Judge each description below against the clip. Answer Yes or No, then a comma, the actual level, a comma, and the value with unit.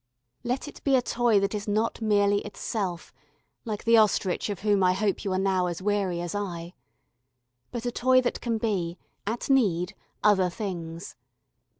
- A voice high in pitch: Yes, high, 205 Hz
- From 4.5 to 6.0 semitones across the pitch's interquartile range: No, average, 3.6 semitones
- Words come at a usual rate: Yes, average, 175 wpm